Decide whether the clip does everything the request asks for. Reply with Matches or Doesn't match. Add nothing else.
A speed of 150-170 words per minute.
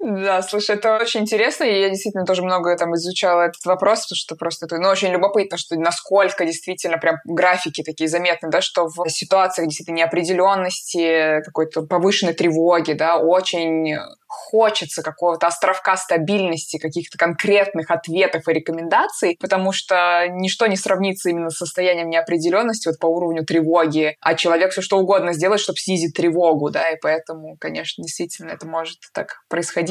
Matches